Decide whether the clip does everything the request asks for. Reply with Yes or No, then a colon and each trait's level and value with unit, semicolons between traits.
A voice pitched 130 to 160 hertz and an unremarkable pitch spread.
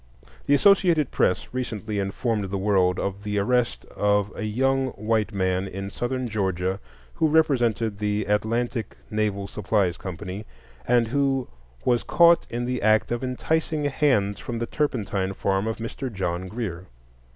No: low, 110 Hz; average, 4.2 semitones